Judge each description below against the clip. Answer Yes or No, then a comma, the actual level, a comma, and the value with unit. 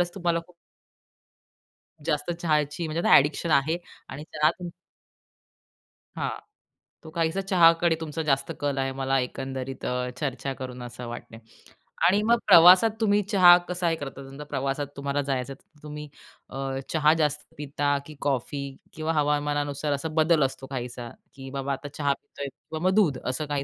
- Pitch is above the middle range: No, medium, 145 Hz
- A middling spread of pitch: Yes, average, 3.2 semitones